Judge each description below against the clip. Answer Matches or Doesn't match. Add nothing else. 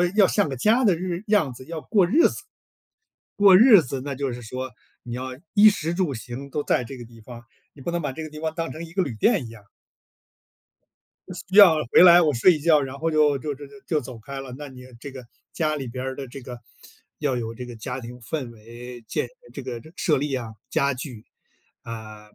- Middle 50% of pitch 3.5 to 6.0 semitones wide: Matches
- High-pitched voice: Doesn't match